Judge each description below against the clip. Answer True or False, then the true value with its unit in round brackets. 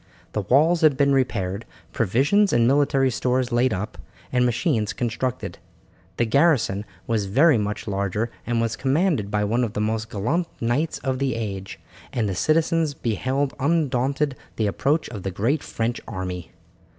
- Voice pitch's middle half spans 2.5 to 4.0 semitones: False (4.8 semitones)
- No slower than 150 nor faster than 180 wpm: True (160 wpm)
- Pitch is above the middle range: False (120 Hz)